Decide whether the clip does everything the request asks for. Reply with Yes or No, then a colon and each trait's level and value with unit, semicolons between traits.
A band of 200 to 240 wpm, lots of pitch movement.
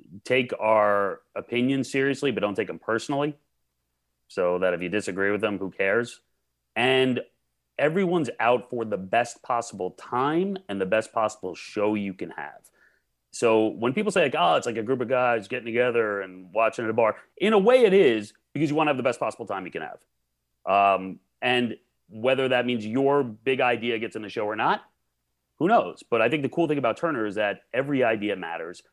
Yes: fast, 205 wpm; wide, 5.8 semitones